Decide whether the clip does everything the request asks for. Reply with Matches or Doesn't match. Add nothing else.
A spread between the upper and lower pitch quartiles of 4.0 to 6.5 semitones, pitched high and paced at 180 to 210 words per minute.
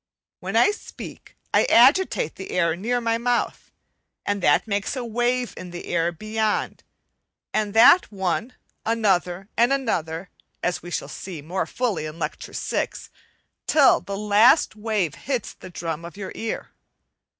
Doesn't match